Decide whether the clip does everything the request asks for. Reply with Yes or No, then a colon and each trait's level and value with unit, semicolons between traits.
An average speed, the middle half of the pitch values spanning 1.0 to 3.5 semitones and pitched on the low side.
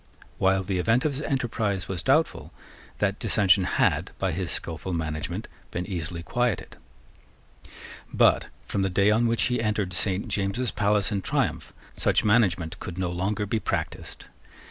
Yes: average, 155 wpm; average, 3.2 semitones; low, 100 Hz